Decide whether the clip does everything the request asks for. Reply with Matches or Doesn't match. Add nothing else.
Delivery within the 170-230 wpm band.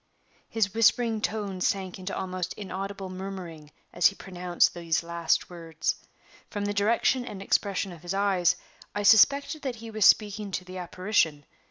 Doesn't match